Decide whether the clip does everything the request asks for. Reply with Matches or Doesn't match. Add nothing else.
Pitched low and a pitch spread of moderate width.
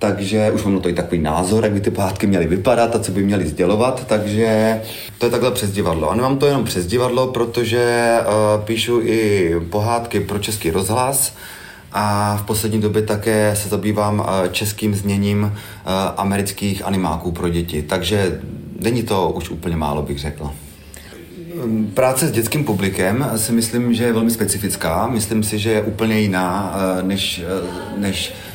Matches